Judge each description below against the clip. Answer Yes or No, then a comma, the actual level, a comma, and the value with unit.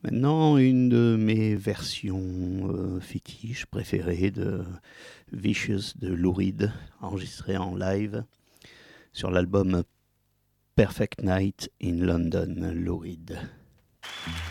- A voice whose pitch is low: Yes, very low, 95 Hz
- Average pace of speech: No, slow, 95 wpm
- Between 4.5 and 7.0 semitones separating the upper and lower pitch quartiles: No, average, 2.8 semitones